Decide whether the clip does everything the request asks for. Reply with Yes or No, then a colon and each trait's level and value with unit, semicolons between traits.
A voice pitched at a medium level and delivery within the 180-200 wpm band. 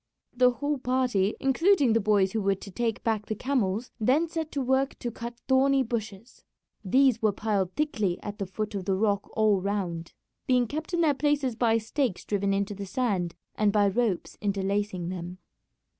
No: high, 220 Hz; average, 185 wpm